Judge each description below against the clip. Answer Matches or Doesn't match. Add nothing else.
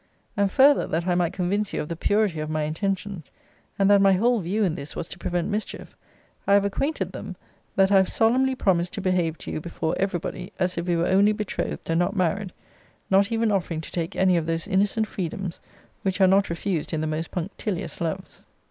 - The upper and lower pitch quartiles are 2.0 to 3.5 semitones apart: Matches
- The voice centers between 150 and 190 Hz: Matches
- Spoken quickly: Matches